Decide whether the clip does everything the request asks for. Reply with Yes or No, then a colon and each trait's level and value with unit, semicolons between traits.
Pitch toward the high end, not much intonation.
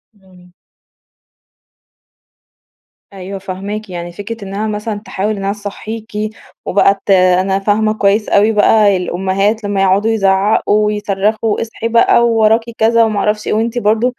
Yes: high, 205 Hz; narrow, 2.1 semitones